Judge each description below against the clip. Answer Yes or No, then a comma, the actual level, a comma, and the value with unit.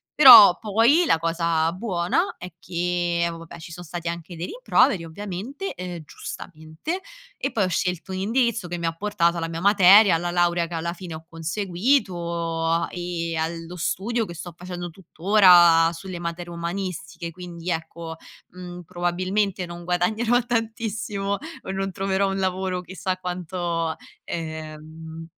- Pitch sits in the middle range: Yes, medium, 175 Hz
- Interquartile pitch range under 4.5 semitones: Yes, narrow, 2.5 semitones